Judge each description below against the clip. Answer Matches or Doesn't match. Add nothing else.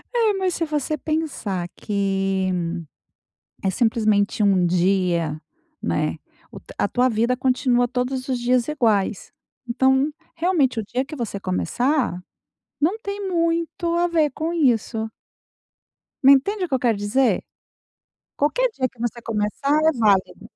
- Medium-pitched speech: Doesn't match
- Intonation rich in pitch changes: Matches